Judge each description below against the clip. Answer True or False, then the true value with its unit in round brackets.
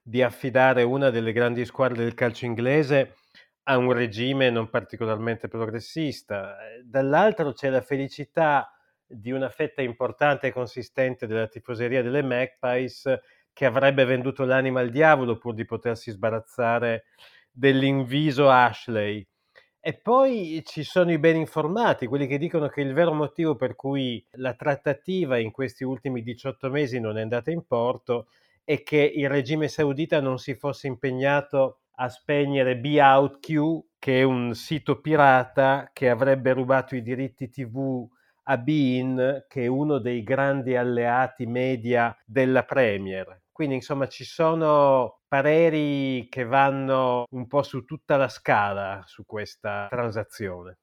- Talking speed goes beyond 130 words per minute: True (140 wpm)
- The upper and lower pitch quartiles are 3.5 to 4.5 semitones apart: False (2.7 semitones)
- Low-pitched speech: True (130 Hz)